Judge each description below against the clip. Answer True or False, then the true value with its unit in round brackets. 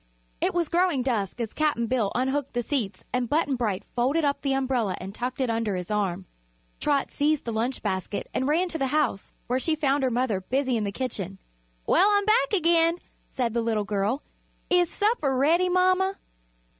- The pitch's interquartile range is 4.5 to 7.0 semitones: True (5.5 semitones)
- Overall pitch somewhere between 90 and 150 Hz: False (260 Hz)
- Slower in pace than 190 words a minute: False (195 wpm)